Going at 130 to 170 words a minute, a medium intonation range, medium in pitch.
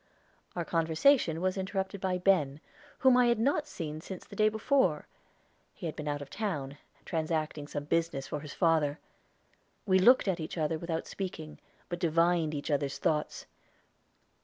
Yes: average, 160 wpm; average, 3.9 semitones; medium, 165 Hz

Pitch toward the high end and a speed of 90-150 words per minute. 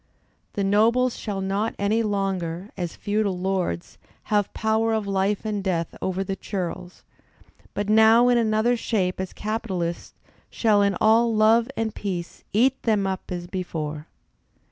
Yes: high, 200 Hz; average, 145 wpm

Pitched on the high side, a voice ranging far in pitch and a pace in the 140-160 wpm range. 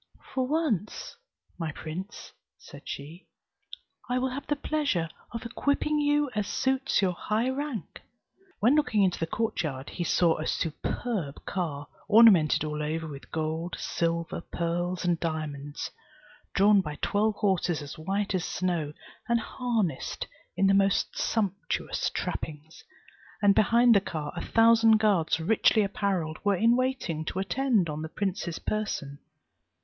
Yes: high, 195 Hz; wide, 5.9 semitones; average, 145 wpm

